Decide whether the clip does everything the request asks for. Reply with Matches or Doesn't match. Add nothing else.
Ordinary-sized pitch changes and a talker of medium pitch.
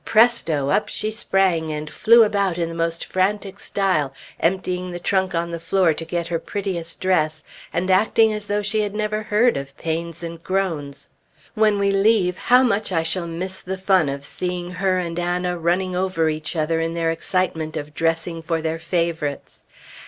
Matches